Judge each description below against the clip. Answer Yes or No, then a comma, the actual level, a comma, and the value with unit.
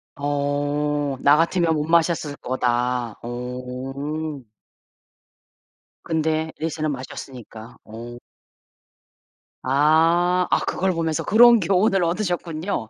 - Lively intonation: No, average, 4.4 semitones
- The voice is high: No, medium, 150 Hz